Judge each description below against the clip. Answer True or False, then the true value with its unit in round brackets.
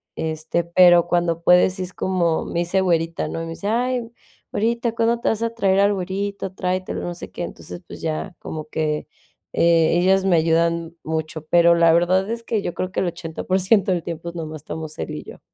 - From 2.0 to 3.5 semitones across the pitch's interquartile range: True (2.7 semitones)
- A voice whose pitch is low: False (175 Hz)